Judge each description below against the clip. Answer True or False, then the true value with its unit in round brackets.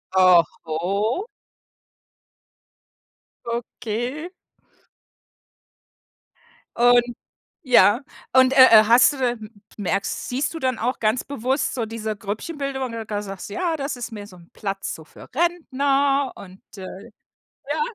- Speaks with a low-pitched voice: False (240 Hz)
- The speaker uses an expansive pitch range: False (4.8 semitones)